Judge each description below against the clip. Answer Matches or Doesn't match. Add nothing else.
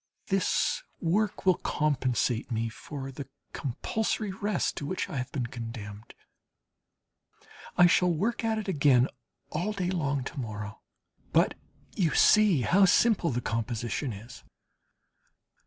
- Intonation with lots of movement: Matches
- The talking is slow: Matches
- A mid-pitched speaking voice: Matches